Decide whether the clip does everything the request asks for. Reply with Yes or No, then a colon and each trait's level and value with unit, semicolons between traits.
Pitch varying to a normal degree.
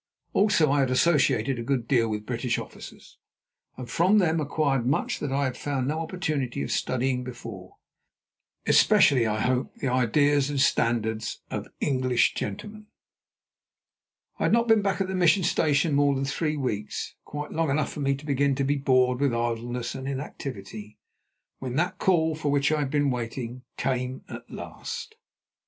Yes: average, 3.6 semitones